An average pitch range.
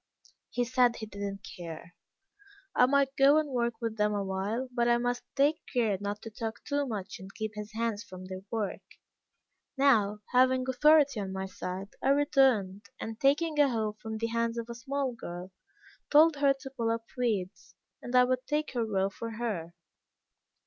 Yes: average, 4.4 semitones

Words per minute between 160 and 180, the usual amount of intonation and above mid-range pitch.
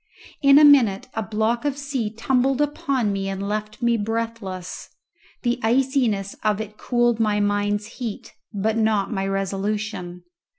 No: average, 145 wpm; average, 3.0 semitones; high, 220 Hz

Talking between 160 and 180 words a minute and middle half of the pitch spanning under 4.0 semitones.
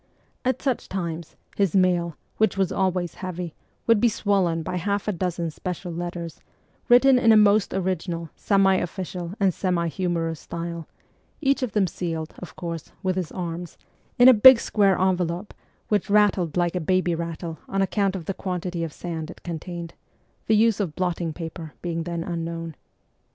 Yes: average, 170 wpm; average, 2.7 semitones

